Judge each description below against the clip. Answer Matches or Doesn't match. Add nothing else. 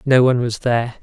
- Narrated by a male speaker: Matches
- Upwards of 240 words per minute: Doesn't match